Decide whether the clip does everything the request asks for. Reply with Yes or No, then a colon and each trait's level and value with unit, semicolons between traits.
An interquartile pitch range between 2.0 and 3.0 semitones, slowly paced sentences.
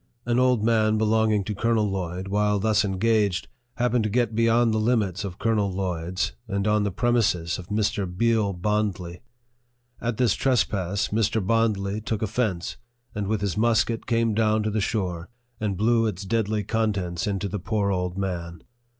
No: narrow, 2.6 semitones; average, 170 wpm